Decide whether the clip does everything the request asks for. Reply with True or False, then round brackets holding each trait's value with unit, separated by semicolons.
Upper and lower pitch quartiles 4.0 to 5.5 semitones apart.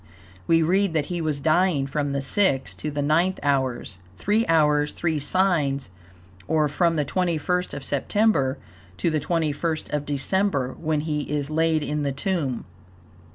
False (3.3 semitones)